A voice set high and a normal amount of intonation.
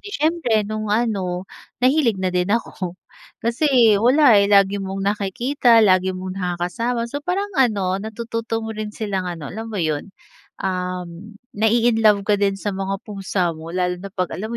Yes: high, 205 Hz; average, 3.7 semitones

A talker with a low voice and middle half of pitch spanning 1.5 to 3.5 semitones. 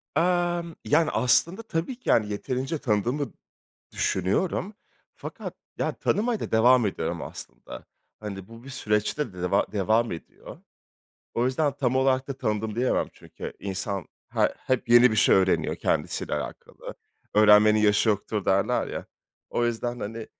No: low, 115 Hz; average, 4.5 semitones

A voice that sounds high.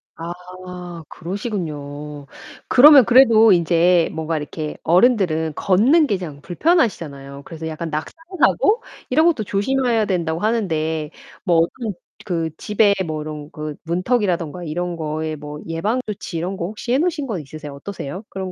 No: medium, 175 Hz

